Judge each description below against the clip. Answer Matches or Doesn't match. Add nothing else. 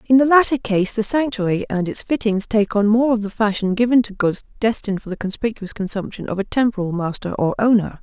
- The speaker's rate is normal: Doesn't match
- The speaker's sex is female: Matches